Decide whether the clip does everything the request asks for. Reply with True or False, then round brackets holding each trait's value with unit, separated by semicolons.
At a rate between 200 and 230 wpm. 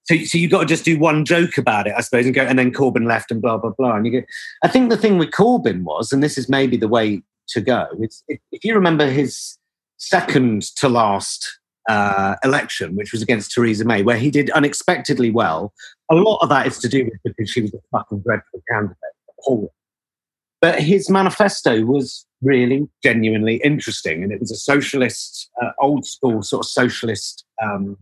True (205 wpm)